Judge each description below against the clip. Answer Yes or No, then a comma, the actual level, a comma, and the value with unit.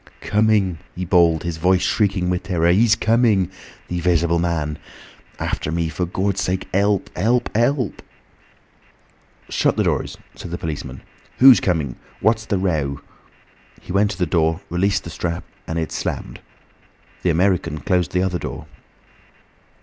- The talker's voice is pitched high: No, very low, 90 Hz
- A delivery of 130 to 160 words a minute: Yes, average, 150 wpm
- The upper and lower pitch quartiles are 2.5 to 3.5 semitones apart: Yes, average, 3.2 semitones